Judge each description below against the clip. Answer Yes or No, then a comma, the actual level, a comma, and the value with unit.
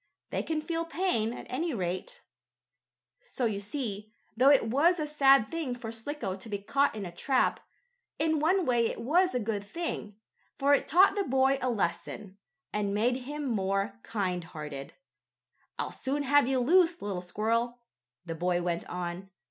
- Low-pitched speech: No, high, 240 Hz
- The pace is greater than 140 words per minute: Yes, average, 170 wpm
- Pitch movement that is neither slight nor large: No, wide, 6.6 semitones